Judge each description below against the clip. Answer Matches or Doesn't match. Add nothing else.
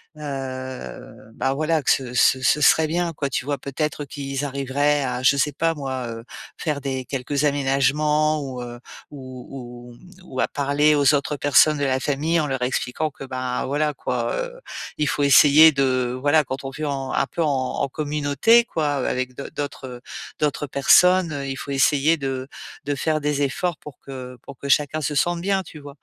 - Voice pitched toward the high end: Doesn't match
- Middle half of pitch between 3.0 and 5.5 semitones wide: Doesn't match